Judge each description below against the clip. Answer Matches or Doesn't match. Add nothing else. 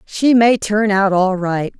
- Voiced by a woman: Matches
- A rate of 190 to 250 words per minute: Matches